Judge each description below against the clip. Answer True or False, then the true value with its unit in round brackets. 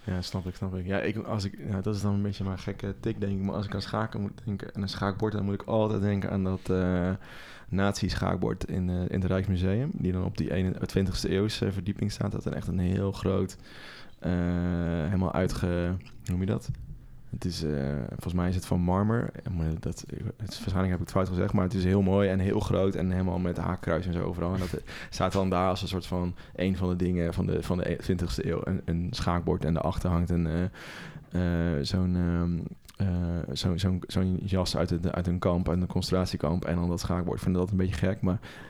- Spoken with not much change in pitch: True (1.9 semitones)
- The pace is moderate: False (235 wpm)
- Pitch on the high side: False (95 Hz)